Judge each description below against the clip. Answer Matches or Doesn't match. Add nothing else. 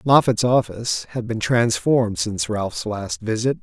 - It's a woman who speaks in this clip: Doesn't match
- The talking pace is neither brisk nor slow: Matches